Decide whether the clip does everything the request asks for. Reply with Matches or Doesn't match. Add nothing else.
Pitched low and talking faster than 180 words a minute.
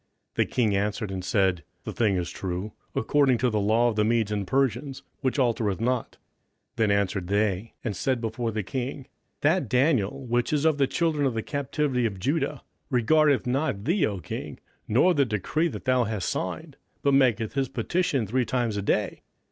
Matches